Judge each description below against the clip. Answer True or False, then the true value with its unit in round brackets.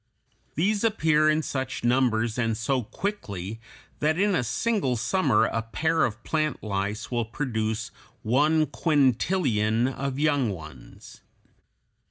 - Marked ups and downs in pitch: True (5.7 semitones)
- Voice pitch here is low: True (130 Hz)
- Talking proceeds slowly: True (125 wpm)